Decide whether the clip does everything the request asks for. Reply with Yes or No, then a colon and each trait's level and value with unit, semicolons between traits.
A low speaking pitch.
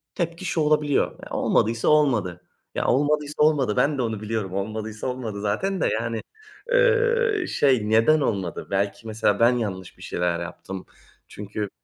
Yes: low, 115 Hz